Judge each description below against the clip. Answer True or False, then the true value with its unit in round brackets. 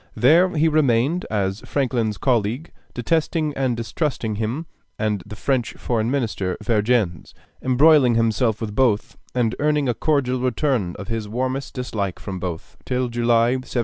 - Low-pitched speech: True (120 Hz)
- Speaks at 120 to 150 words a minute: True (145 wpm)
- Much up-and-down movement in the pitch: False (3.9 semitones)